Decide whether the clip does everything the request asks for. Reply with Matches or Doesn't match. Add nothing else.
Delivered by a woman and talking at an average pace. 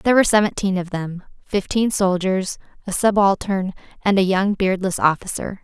Matches